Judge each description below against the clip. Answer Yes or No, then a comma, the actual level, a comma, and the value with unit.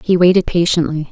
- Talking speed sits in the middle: Yes, average, 160 wpm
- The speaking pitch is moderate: Yes, medium, 175 Hz